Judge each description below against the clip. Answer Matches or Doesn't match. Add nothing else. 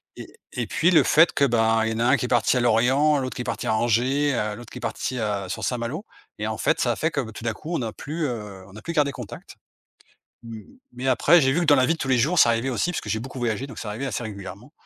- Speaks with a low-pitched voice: Matches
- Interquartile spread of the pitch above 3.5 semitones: Matches